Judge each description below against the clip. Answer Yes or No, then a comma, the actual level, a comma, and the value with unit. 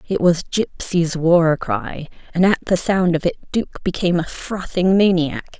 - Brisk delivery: No, average, 170 wpm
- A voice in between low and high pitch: Yes, medium, 170 Hz